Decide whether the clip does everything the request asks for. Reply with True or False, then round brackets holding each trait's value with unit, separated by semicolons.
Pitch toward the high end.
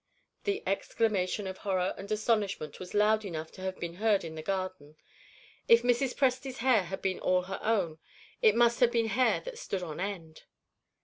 True (200 Hz)